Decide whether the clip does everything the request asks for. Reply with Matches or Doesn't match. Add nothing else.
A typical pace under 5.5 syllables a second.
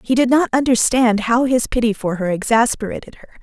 Doesn't match